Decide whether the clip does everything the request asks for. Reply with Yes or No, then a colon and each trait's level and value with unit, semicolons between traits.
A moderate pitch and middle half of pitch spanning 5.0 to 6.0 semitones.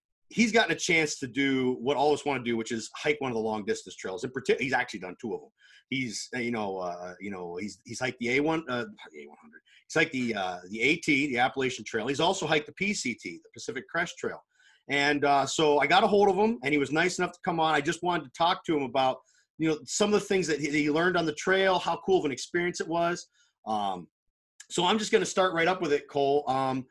Yes: medium, 150 Hz; wide, 5.6 semitones